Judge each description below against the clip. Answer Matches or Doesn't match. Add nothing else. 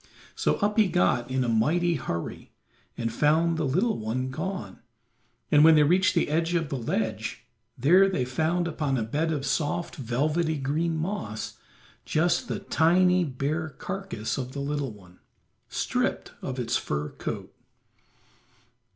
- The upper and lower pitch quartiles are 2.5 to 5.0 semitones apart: Doesn't match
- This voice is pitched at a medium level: Matches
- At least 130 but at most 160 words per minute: Matches